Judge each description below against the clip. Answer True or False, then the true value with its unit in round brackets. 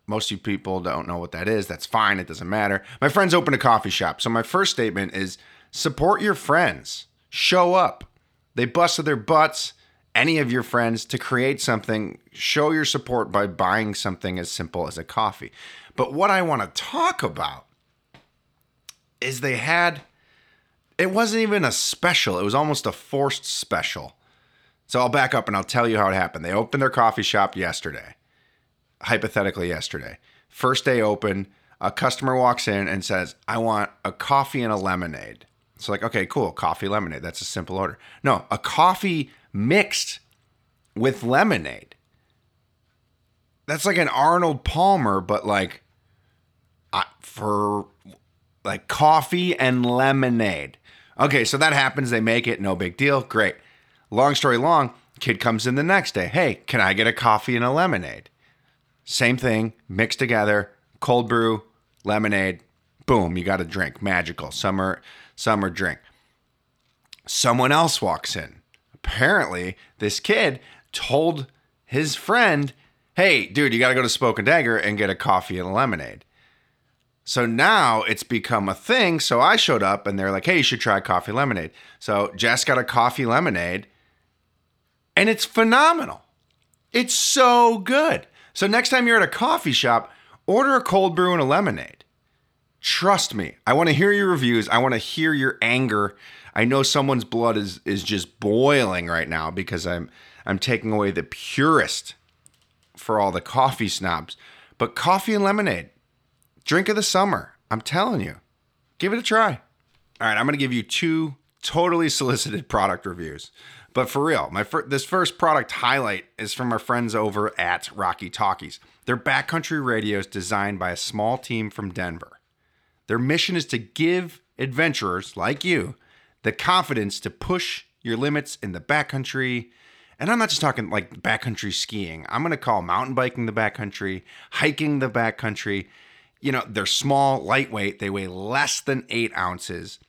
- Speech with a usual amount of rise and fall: False (6.2 semitones)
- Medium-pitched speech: False (120 Hz)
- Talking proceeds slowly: False (165 wpm)